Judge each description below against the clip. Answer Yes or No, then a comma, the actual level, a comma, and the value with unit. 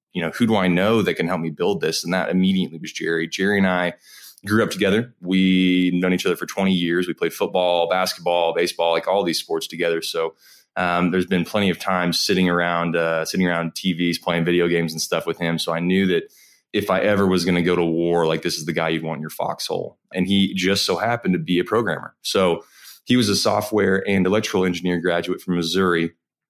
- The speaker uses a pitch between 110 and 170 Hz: No, very low, 90 Hz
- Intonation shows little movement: Yes, narrow, 1.9 semitones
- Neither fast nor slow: No, fast, 235 wpm